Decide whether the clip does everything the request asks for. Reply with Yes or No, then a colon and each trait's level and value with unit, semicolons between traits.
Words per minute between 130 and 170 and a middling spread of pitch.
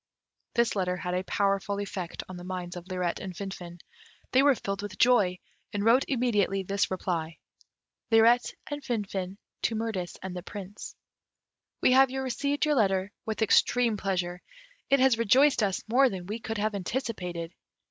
Yes: average, 165 wpm; average, 4.4 semitones